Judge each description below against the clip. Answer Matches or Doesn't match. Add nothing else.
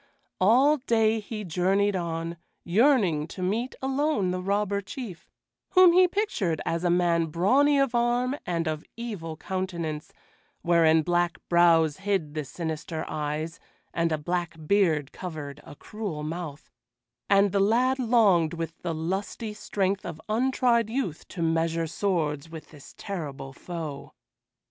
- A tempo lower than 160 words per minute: Matches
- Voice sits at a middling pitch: Matches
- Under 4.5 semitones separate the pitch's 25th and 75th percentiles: Doesn't match